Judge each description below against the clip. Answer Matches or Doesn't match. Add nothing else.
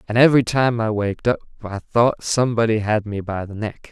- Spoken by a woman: Doesn't match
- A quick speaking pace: Matches